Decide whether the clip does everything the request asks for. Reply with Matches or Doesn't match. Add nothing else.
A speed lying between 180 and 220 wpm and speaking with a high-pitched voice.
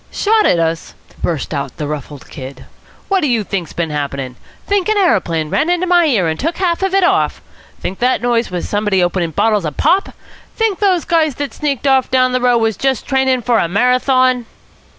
Matches